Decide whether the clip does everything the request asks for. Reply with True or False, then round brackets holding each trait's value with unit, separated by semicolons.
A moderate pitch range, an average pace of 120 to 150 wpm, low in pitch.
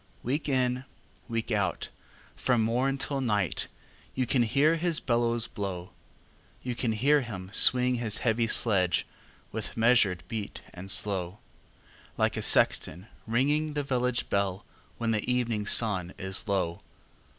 True (4.0 semitones; 140 wpm; 115 Hz)